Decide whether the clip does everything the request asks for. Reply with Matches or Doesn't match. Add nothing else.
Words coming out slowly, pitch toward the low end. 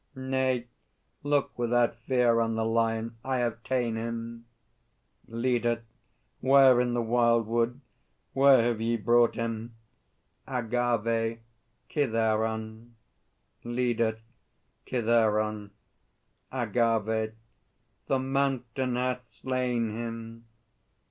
Matches